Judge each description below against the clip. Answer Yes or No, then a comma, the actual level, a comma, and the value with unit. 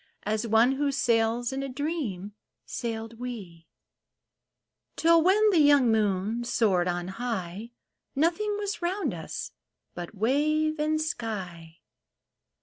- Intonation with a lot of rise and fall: Yes, wide, 7.0 semitones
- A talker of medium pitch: No, high, 235 Hz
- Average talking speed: No, slow, 120 wpm